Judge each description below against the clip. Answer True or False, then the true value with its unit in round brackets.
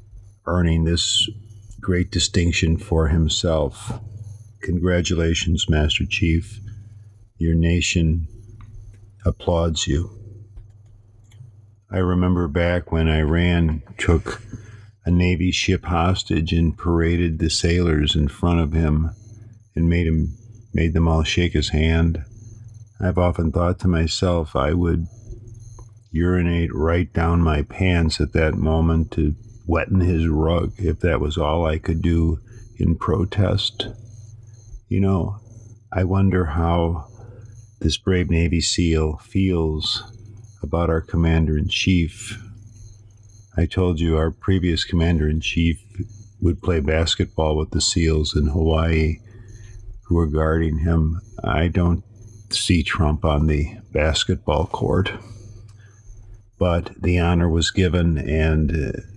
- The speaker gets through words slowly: True (120 wpm)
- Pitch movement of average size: True (4.2 semitones)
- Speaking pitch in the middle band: False (90 Hz)